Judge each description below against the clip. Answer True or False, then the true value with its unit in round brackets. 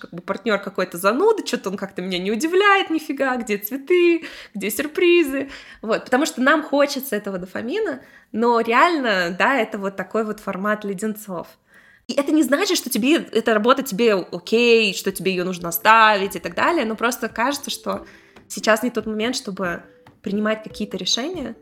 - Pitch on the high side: True (225 Hz)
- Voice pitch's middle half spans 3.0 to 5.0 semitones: False (5.6 semitones)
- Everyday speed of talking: False (170 wpm)